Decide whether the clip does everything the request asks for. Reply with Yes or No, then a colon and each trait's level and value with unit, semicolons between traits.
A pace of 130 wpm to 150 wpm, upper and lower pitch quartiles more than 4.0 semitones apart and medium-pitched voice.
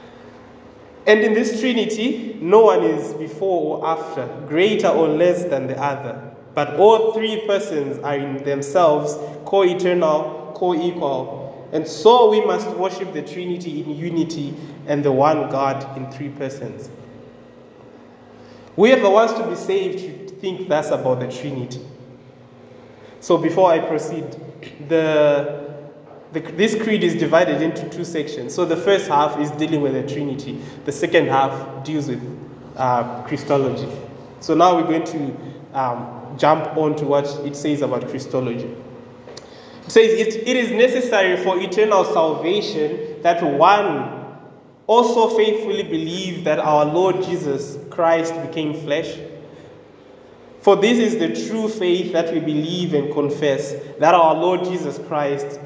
Yes: average, 145 wpm; average, 4.6 semitones; medium, 155 Hz